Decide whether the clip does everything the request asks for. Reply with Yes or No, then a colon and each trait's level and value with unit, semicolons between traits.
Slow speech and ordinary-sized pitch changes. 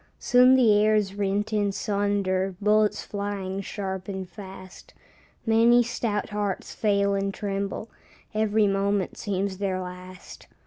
No: slow, 130 wpm; narrow, 1.6 semitones